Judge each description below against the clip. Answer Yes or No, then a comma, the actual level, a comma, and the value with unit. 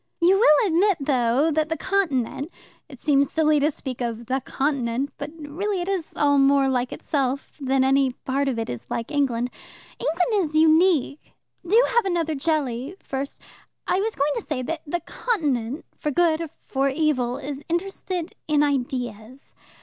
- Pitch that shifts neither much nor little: Yes, average, 3.8 semitones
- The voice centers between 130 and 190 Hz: No, very high, 290 Hz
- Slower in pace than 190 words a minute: Yes, average, 170 wpm